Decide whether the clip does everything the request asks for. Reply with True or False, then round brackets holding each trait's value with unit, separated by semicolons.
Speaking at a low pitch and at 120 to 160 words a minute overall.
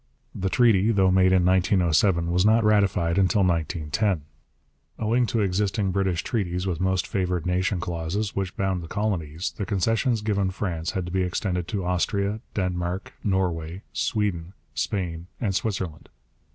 True (95 Hz; 150 wpm)